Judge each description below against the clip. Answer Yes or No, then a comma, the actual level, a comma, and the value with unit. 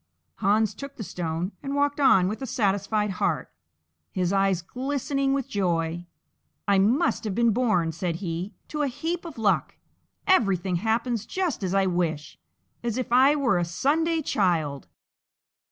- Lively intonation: Yes, wide, 7.0 semitones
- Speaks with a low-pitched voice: No, high, 210 Hz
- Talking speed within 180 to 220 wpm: No, average, 155 wpm